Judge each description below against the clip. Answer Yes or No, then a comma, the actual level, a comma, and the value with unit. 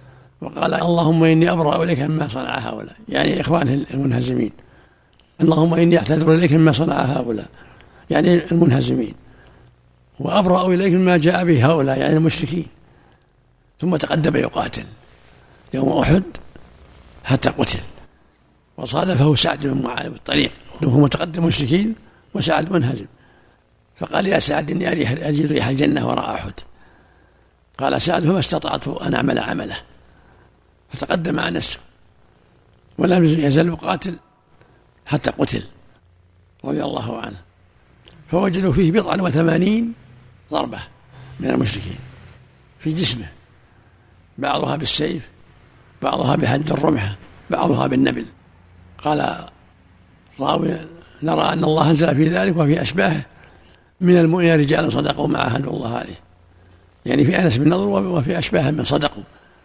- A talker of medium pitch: Yes, medium, 145 Hz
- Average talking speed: Yes, average, 115 wpm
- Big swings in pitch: Yes, wide, 8.8 semitones